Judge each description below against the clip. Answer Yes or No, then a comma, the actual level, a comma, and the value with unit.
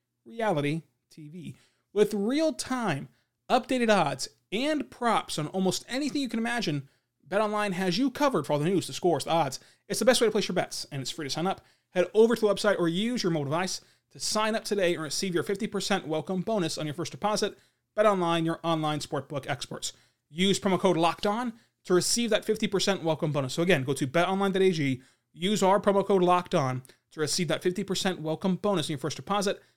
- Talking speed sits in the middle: No, fast, 210 wpm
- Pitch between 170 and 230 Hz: Yes, medium, 185 Hz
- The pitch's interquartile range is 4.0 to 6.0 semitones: Yes, average, 4.9 semitones